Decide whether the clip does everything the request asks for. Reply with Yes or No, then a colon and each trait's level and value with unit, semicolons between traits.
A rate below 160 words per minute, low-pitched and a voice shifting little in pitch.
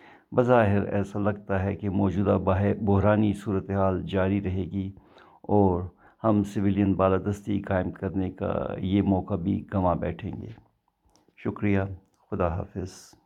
Yes: average, 125 wpm; low, 100 Hz; narrow, 1.2 semitones